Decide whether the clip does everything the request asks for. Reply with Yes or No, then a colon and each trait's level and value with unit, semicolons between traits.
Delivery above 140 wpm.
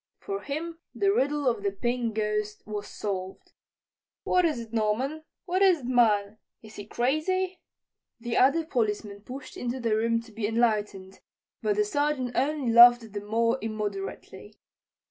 Yes: average, 155 wpm